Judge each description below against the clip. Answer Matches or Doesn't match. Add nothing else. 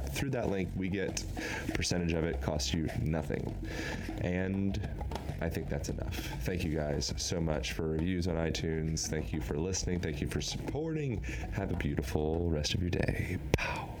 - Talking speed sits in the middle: Matches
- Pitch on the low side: Matches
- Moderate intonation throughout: Matches